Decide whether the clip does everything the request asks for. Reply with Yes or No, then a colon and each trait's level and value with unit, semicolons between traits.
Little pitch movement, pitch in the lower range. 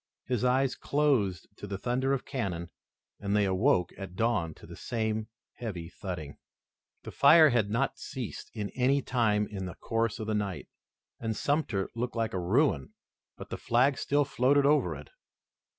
No: average, 4.9 semitones; low, 115 Hz